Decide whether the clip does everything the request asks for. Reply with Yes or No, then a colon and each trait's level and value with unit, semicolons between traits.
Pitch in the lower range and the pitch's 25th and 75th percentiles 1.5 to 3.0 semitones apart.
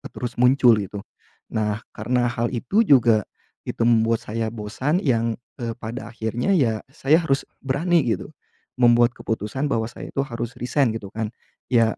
Yes: low, 120 Hz; average, 2.7 semitones